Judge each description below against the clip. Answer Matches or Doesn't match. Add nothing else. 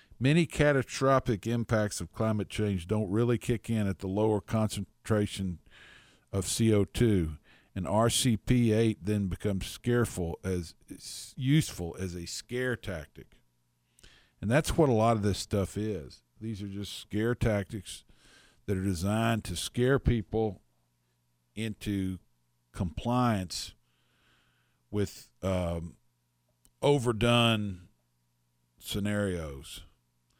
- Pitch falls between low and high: Doesn't match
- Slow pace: Matches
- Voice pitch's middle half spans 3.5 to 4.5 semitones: Doesn't match